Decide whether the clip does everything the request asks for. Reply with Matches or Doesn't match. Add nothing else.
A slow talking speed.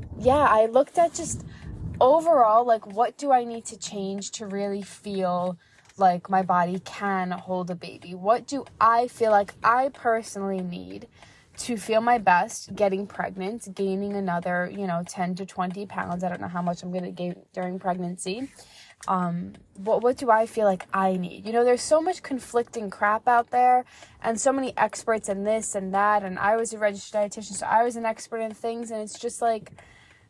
Doesn't match